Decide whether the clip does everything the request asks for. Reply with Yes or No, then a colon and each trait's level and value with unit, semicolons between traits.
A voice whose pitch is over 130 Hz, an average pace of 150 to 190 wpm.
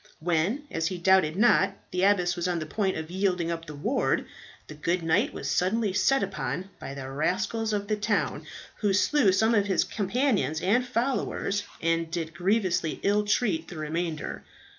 Yes: medium, 185 Hz; average, 180 wpm